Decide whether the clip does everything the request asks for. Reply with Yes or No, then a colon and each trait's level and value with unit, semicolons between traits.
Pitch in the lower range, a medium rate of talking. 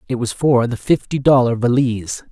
Yes: low, 125 Hz; average, 180 wpm